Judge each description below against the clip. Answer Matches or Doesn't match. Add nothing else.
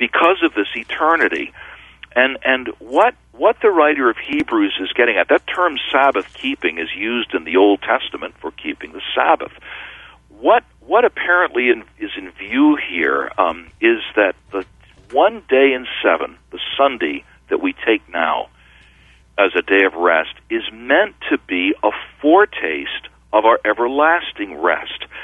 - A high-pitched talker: Matches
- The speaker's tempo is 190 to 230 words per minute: Doesn't match